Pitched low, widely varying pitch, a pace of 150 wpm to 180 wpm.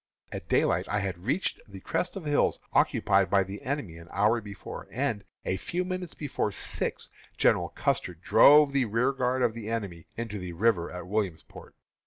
Yes: low, 110 Hz; wide, 6.0 semitones; average, 175 wpm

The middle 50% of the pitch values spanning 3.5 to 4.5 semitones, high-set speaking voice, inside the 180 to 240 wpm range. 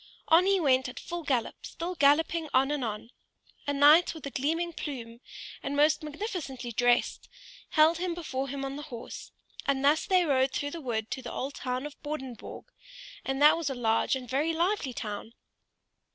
Yes: average, 3.8 semitones; very high, 285 Hz; average, 185 wpm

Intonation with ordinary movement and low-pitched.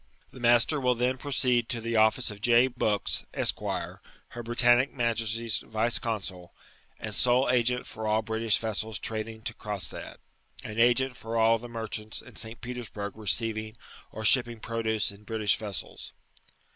No: narrow, 1.8 semitones; low, 115 Hz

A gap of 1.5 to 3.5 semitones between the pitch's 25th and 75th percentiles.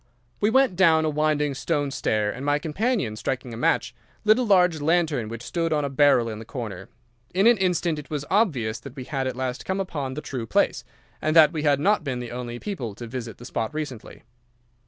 No: wide, 5.4 semitones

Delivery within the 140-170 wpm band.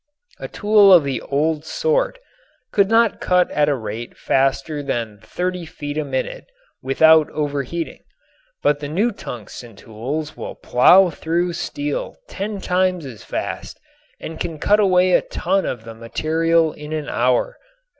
Yes: average, 150 wpm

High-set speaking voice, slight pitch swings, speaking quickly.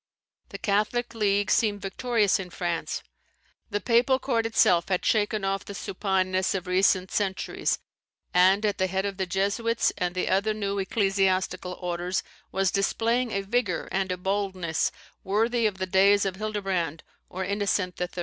No: high, 195 Hz; narrow, 2.1 semitones; average, 160 wpm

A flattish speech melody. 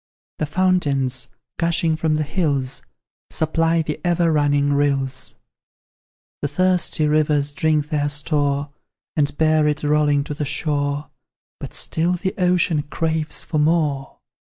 Yes: narrow, 2.1 semitones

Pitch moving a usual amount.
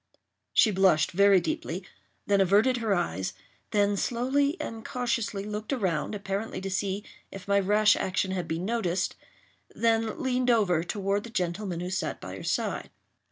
Yes: average, 3.2 semitones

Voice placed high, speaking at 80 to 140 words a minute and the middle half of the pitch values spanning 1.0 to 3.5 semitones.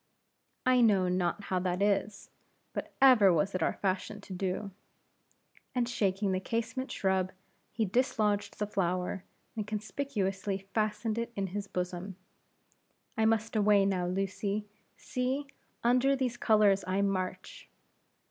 Yes: high, 200 Hz; slow, 135 wpm; average, 2.9 semitones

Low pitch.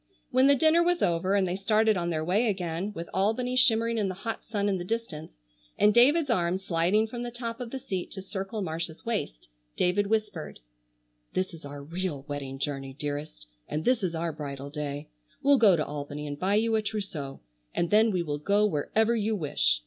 No: high, 190 Hz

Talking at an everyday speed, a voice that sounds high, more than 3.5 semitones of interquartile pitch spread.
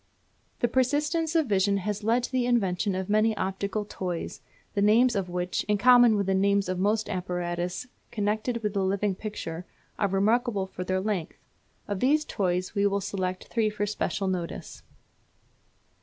No: average, 170 wpm; high, 200 Hz; average, 3.0 semitones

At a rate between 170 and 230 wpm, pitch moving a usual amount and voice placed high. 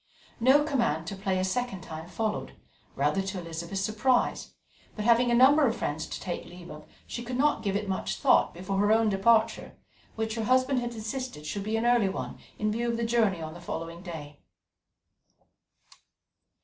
Yes: average, 190 wpm; average, 4.9 semitones; high, 210 Hz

